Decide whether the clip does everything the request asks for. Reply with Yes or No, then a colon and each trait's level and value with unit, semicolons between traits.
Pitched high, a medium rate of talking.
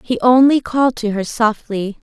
Yes: high, 230 Hz; average, 170 wpm